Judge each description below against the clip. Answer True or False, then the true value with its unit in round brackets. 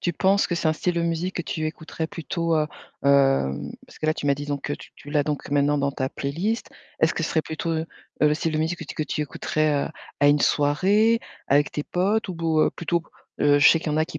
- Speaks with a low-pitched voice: False (155 Hz)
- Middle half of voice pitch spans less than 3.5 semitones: True (2.6 semitones)